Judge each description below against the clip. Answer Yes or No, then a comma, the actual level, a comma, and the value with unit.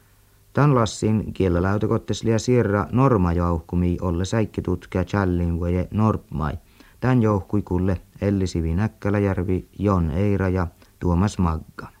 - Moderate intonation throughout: Yes, average, 3.0 semitones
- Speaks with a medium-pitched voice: No, very low, 95 Hz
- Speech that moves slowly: Yes, slow, 90 wpm